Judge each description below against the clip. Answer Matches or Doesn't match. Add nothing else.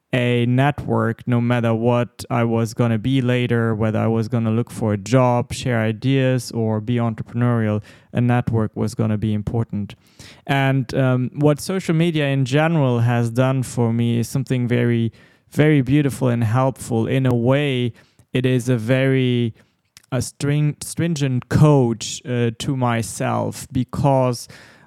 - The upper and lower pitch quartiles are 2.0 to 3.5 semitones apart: Matches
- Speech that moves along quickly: Doesn't match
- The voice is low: Matches